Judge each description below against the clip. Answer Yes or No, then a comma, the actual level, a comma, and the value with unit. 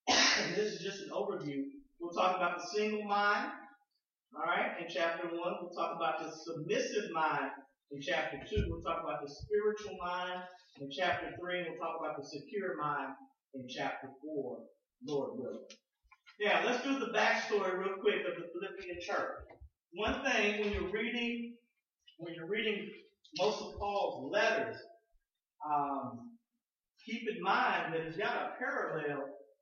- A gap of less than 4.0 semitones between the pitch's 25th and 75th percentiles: No, average, 5.0 semitones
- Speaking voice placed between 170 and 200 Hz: Yes, medium, 185 Hz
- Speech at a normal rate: Yes, average, 160 wpm